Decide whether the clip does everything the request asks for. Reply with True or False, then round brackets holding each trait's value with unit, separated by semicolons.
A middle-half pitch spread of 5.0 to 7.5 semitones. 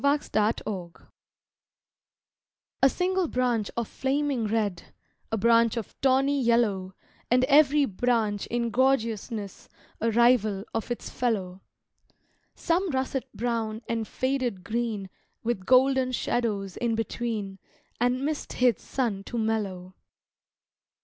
False (3.5 semitones)